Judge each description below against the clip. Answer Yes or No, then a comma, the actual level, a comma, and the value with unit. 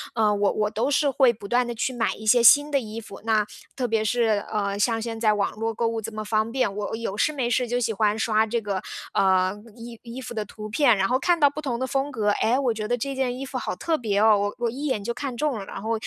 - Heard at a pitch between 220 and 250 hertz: Yes, high, 225 Hz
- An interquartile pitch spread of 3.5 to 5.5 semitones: No, average, 2.9 semitones